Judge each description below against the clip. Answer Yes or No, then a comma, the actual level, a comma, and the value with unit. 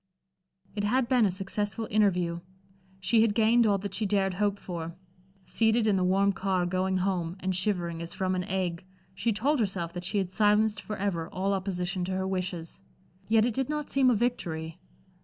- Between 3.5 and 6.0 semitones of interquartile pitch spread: No, average, 2.9 semitones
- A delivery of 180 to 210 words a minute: Yes, average, 190 wpm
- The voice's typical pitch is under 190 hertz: No, high, 195 Hz